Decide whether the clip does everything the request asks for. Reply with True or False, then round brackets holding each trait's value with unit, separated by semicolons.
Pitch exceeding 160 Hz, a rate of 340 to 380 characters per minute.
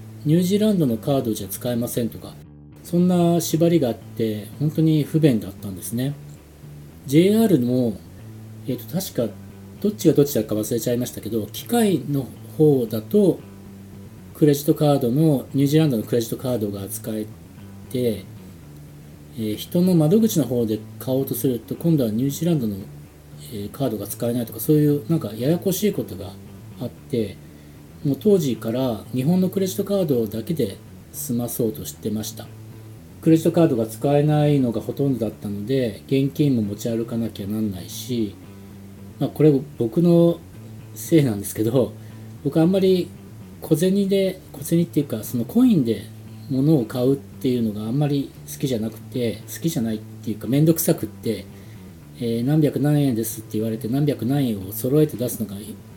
False (120 Hz; 355 characters per minute)